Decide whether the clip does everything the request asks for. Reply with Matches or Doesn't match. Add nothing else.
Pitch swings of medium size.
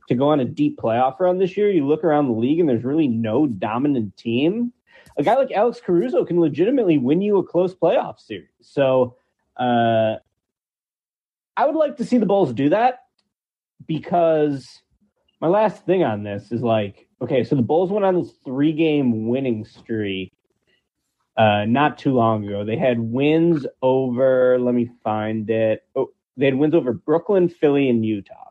Doesn't match